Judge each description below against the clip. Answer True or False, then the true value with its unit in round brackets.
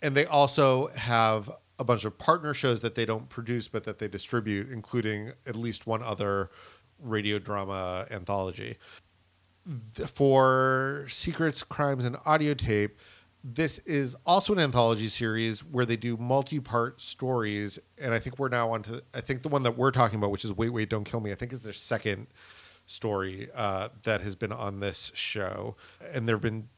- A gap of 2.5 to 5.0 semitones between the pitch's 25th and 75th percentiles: True (3.8 semitones)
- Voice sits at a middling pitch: False (115 Hz)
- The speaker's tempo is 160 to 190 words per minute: True (185 wpm)